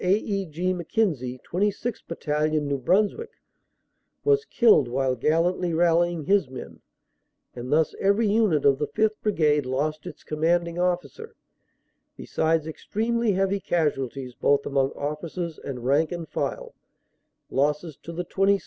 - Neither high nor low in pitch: Yes, medium, 170 Hz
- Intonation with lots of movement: No, average, 5.0 semitones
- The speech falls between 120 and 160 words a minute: Yes, average, 140 wpm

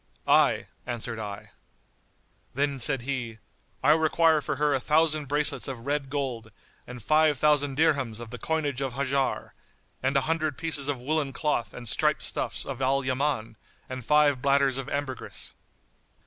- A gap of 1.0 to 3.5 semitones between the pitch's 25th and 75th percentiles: Yes, average, 2.8 semitones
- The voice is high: No, medium, 140 Hz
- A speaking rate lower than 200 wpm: Yes, average, 160 wpm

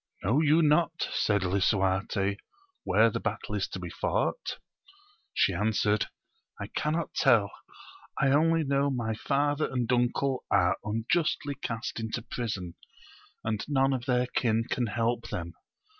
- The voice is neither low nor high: No, low, 120 Hz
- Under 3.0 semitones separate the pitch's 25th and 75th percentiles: No, average, 5.1 semitones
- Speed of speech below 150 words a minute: Yes, average, 140 wpm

